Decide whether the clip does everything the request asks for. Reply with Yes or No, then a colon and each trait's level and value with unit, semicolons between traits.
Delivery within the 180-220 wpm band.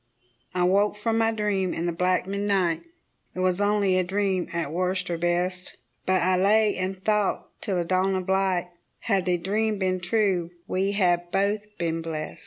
Yes: average, 185 wpm